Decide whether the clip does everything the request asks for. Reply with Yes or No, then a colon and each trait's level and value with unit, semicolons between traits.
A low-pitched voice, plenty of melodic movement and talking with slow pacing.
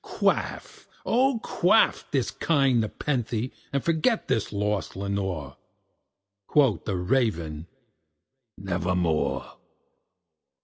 Yes: low, 105 Hz; wide, 7.1 semitones; slow, 85 wpm